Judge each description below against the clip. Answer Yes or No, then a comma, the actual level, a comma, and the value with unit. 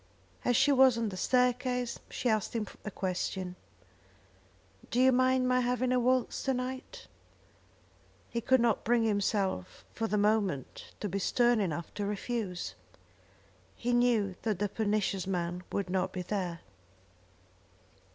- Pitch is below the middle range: No, high, 220 Hz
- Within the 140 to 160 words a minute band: Yes, average, 145 wpm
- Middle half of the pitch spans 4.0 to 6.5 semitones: Yes, average, 4.3 semitones